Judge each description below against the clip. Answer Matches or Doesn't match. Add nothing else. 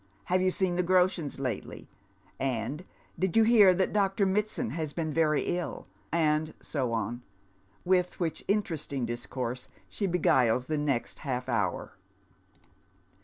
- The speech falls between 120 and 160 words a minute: Matches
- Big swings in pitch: Matches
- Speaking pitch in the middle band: Matches